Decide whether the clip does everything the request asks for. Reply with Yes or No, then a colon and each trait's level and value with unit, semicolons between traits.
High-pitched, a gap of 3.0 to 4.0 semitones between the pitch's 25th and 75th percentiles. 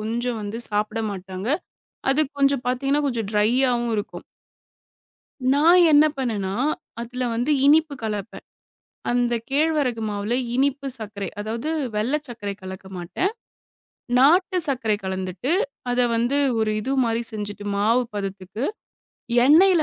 No: high, 235 Hz; average, 4.9 semitones